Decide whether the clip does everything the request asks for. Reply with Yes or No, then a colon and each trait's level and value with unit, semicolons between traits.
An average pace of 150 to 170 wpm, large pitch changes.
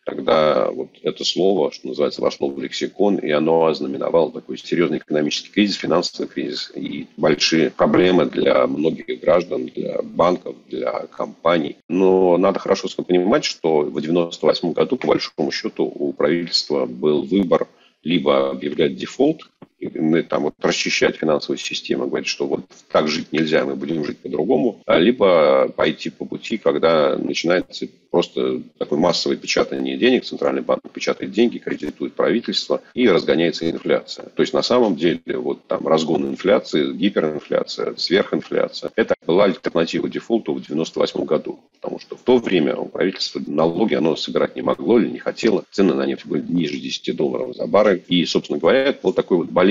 Yes: fast, 160 wpm; wide, 6.1 semitones